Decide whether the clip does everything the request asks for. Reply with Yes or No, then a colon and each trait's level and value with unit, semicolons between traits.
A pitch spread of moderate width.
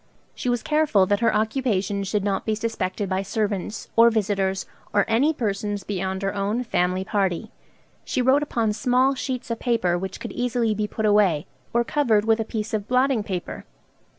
Yes: average, 3.3 semitones